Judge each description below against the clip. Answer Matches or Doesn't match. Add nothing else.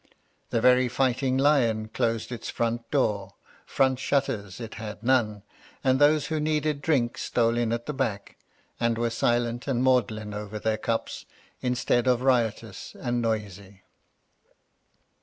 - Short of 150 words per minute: Matches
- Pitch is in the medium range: Doesn't match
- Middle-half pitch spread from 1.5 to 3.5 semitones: Matches